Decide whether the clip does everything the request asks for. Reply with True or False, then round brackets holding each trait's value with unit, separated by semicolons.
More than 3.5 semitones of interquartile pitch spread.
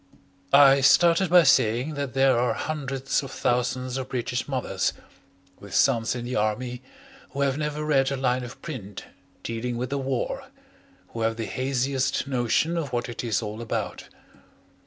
False (2.4 semitones)